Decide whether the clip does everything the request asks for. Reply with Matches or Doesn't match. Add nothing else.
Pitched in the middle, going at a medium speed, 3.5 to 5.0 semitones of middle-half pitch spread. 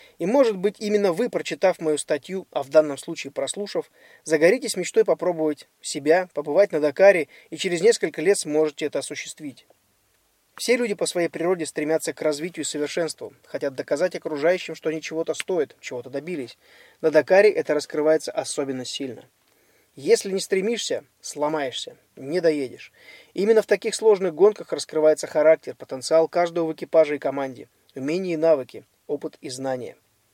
Matches